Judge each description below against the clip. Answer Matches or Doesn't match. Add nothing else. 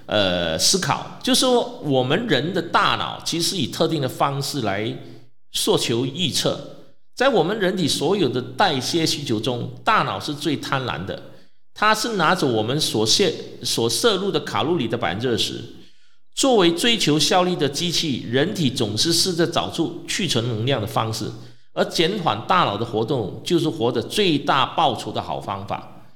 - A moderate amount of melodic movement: Doesn't match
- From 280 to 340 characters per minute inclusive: Doesn't match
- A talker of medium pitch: Matches